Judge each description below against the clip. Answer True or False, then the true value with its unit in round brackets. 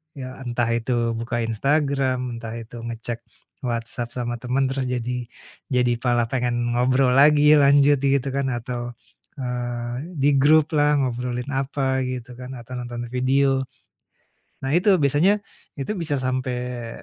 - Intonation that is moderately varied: False (2.3 semitones)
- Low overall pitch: True (125 Hz)